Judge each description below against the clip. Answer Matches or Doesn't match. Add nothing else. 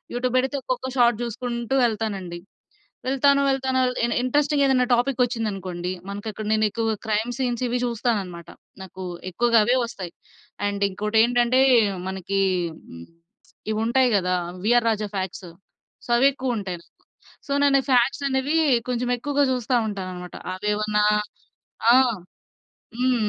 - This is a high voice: Matches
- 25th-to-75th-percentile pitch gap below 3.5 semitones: Doesn't match